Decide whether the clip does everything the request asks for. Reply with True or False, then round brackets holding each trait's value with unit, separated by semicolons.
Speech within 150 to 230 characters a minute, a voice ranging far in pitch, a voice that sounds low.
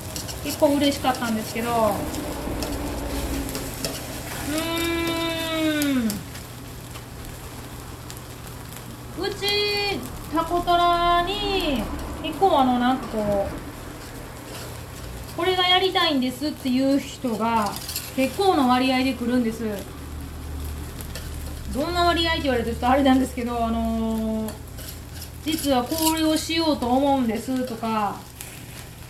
False (200 characters per minute; 6.3 semitones; 265 Hz)